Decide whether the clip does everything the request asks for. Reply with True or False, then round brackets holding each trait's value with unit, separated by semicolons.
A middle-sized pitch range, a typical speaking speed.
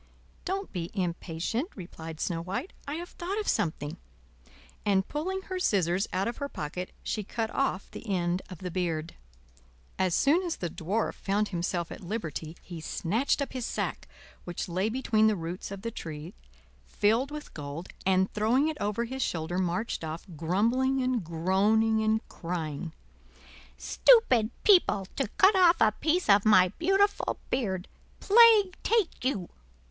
False (7.3 semitones; 160 wpm)